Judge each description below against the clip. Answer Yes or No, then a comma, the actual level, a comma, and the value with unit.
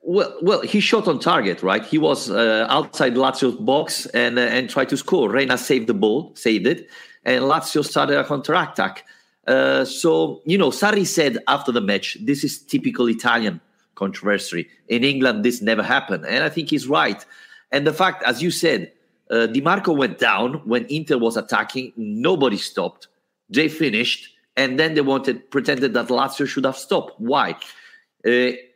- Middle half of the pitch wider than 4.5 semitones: Yes, average, 5.1 semitones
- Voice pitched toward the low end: Yes, low, 130 Hz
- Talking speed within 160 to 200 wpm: Yes, average, 175 wpm